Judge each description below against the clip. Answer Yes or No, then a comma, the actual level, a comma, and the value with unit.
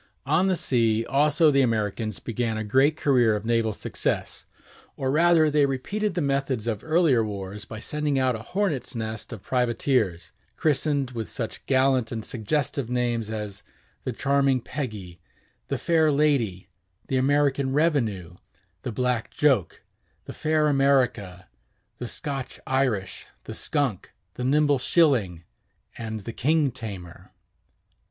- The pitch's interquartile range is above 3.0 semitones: Yes, average, 4.7 semitones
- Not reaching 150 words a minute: Yes, average, 140 wpm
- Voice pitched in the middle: No, low, 130 Hz